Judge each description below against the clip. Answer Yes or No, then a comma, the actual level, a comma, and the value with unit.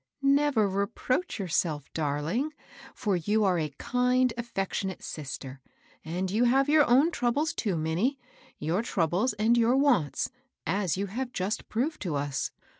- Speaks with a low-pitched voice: No, high, 205 Hz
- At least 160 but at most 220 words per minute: No, average, 150 wpm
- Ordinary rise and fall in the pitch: No, wide, 7.1 semitones